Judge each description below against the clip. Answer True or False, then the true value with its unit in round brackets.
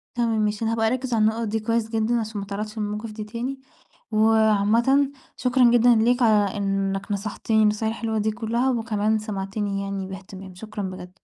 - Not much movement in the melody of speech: True (2.0 semitones)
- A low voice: False (220 Hz)